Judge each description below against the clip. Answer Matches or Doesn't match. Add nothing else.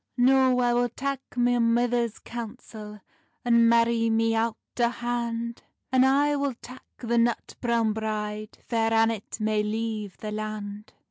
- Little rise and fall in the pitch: Matches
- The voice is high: Matches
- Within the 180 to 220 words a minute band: Doesn't match